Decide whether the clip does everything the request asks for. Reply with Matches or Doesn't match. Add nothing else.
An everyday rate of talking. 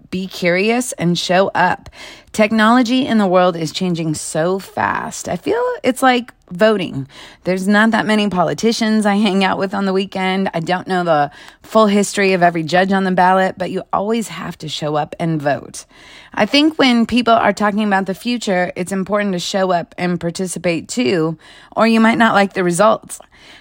Matches